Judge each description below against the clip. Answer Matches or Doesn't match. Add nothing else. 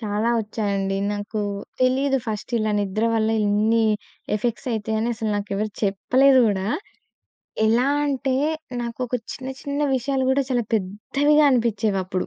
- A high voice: Matches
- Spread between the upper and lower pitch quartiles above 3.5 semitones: Matches